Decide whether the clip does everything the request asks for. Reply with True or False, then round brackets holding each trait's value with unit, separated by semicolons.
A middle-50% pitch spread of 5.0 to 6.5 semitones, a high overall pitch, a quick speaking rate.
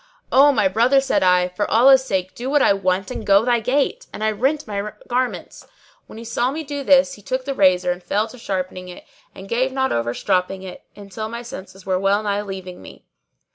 True (5.3 semitones; 210 Hz; 220 wpm)